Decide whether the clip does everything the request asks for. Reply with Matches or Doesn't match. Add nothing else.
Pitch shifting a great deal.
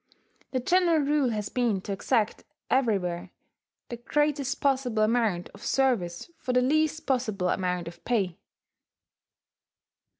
Matches